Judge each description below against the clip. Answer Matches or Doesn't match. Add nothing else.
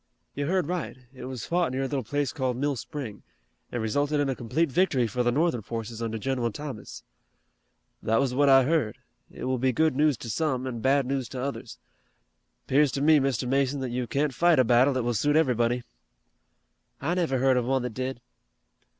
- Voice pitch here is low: Matches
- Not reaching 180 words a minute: Doesn't match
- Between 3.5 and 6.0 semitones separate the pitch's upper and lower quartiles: Doesn't match